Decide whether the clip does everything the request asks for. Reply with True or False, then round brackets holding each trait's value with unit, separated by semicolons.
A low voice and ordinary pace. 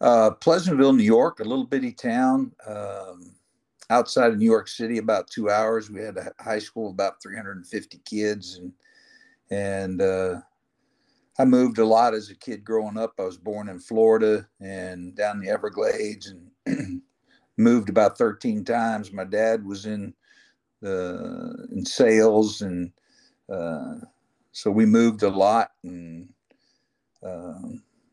True (110 Hz; 150 wpm)